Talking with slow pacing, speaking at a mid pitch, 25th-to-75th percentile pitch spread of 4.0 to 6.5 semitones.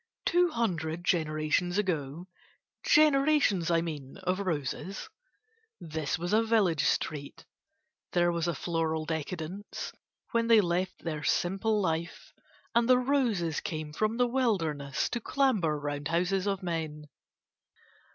Yes: slow, 125 wpm; medium, 175 Hz; average, 5.3 semitones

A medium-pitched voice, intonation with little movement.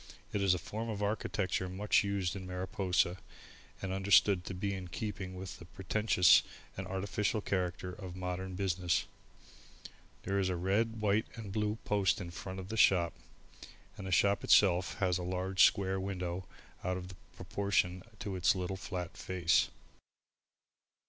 No: very low, 95 Hz; narrow, 1.7 semitones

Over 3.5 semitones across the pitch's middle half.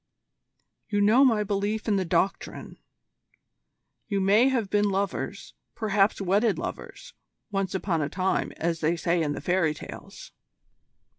No: average, 3.0 semitones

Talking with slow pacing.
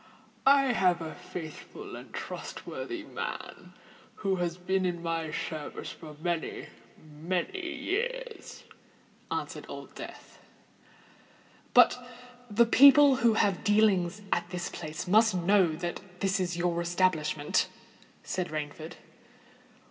Yes: slow, 110 wpm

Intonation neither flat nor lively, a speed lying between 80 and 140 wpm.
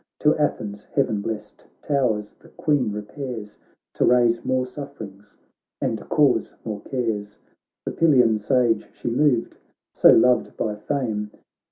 Yes: average, 4.2 semitones; slow, 135 wpm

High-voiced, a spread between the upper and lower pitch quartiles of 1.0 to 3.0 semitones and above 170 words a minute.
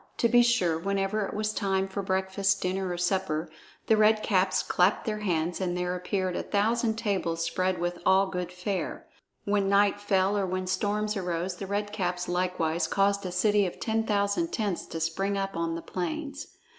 Yes: high, 195 Hz; narrow, 2.5 semitones; average, 190 wpm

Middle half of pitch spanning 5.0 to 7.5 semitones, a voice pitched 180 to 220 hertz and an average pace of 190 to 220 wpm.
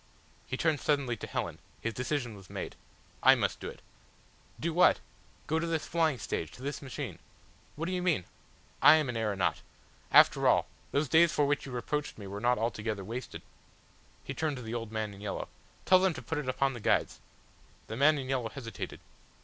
No: wide, 5.4 semitones; low, 130 Hz; average, 200 wpm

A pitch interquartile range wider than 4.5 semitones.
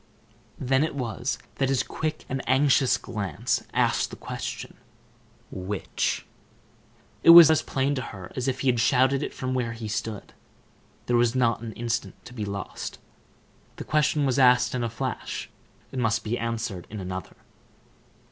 No: average, 3.1 semitones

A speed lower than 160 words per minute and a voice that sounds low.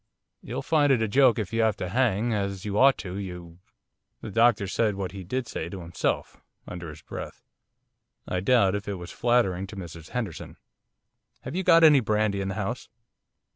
No: average, 200 wpm; low, 100 Hz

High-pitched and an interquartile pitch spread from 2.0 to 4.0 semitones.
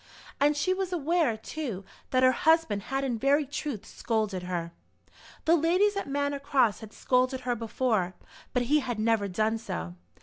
No: very high, 255 Hz; average, 5.2 semitones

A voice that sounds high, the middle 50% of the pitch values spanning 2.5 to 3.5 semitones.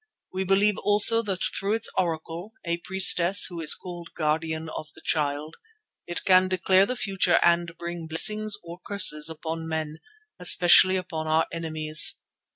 No: medium, 175 Hz; average, 3.1 semitones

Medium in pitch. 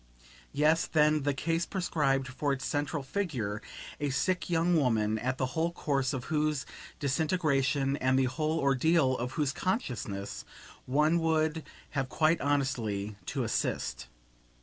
Yes: medium, 145 Hz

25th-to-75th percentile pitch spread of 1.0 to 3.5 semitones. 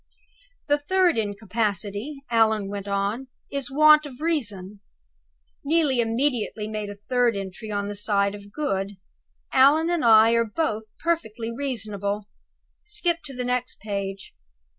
No: wide, 5.5 semitones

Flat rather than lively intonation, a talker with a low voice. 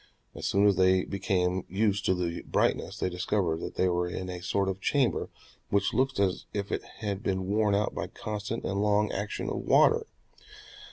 Yes: narrow, 2.0 semitones; low, 100 Hz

